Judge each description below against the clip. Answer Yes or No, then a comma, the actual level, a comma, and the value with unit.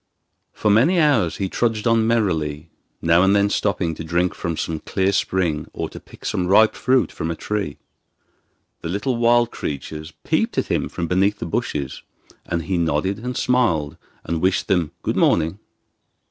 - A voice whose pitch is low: Yes, very low, 95 Hz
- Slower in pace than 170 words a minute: No, average, 175 wpm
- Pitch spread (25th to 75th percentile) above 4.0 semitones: Yes, average, 4.8 semitones